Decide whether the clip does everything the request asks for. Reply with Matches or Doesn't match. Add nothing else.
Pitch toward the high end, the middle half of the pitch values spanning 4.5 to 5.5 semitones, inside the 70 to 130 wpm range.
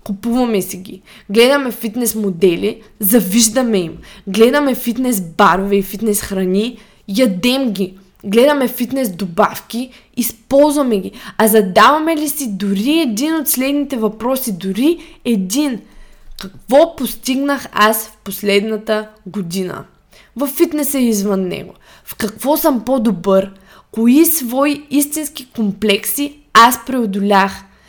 Matches